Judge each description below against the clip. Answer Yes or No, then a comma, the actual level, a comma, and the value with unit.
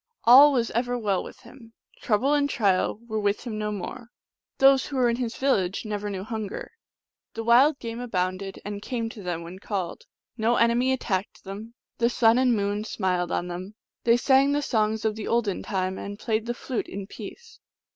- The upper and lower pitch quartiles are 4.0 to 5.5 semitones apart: No, average, 3.4 semitones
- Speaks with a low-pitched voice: No, high, 220 Hz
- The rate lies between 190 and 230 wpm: Yes, average, 195 wpm